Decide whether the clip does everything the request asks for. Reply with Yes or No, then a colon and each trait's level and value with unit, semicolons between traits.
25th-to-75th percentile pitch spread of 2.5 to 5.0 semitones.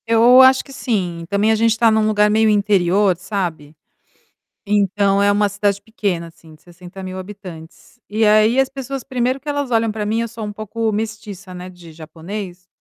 Yes: average, 3.4 semitones